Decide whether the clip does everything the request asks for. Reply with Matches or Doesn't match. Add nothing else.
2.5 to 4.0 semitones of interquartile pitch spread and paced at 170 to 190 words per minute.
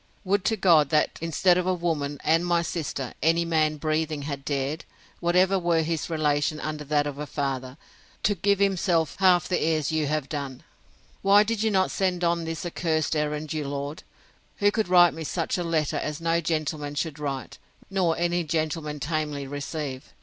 Matches